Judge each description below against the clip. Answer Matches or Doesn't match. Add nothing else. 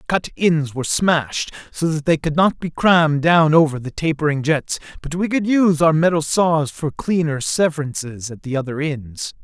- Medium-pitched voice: Matches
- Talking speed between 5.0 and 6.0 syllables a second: Matches